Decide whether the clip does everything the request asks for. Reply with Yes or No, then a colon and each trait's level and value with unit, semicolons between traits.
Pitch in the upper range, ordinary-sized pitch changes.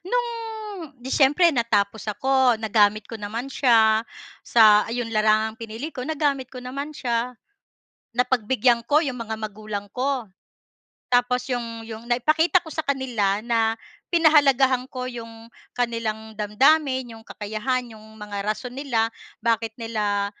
Yes: high, 235 Hz; average, 3.5 semitones